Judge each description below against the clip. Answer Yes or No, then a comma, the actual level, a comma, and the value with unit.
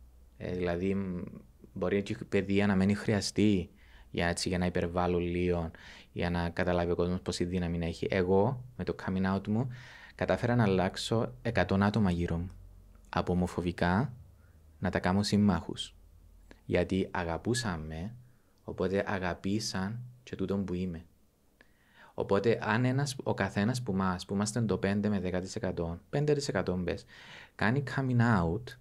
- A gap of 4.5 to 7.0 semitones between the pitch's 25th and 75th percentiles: No, average, 3.2 semitones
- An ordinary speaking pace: Yes, average, 140 wpm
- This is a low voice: Yes, very low, 95 Hz